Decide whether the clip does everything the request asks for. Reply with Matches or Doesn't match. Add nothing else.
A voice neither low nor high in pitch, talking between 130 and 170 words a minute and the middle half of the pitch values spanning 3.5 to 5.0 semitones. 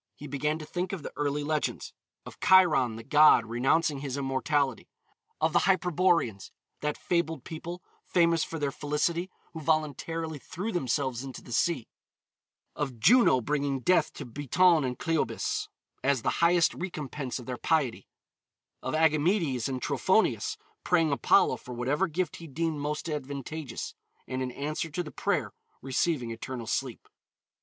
Matches